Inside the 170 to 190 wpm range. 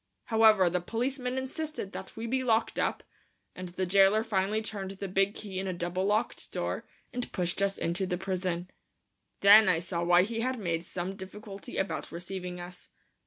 Yes: average, 180 wpm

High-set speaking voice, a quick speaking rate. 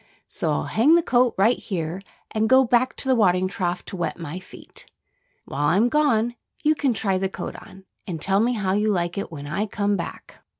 Yes: high, 200 Hz; fast, 215 wpm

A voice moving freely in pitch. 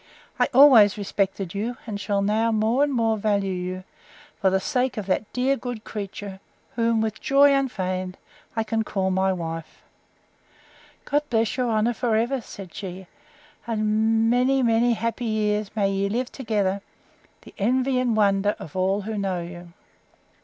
No: average, 3.3 semitones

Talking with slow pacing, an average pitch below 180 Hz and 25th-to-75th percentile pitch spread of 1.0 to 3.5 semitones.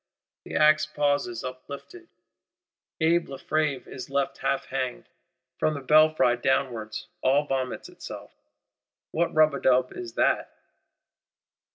Yes: slow, 115 wpm; medium, 140 Hz; average, 3.0 semitones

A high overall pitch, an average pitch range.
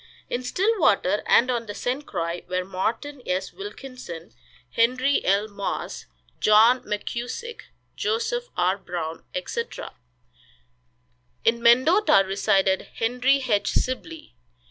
No: high, 235 Hz; wide, 6.1 semitones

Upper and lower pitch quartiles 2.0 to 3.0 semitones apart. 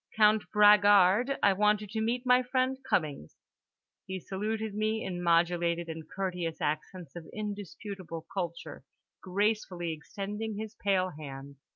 No: average, 3.9 semitones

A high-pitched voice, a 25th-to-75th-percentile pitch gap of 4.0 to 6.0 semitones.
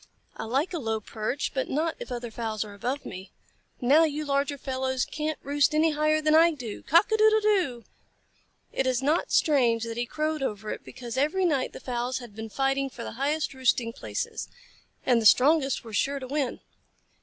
Yes: very high, 270 Hz; average, 4.3 semitones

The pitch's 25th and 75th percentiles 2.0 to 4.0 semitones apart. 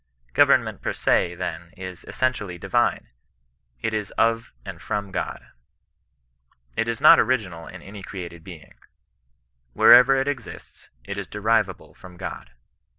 No: average, 4.5 semitones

